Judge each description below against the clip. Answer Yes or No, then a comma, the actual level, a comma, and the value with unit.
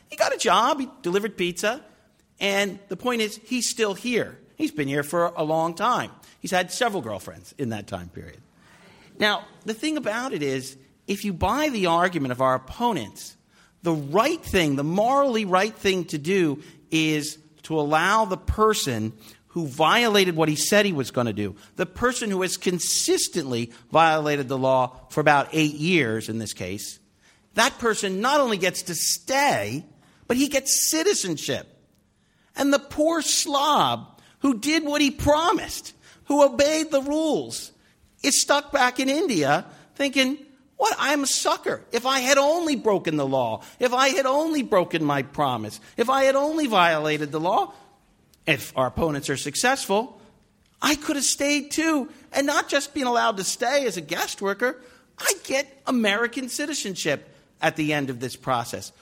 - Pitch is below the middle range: No, high, 205 Hz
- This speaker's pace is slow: No, average, 170 wpm